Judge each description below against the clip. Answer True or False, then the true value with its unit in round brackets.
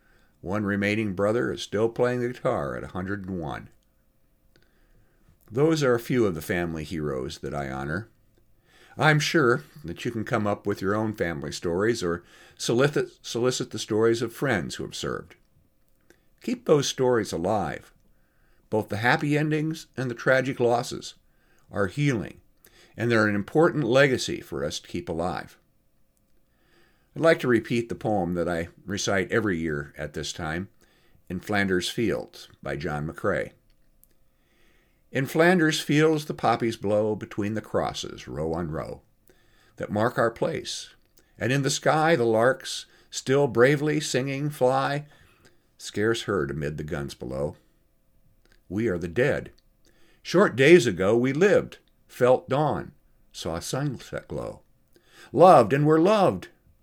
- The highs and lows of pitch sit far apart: True (5.9 semitones)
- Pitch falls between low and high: False (115 Hz)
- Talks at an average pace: True (145 wpm)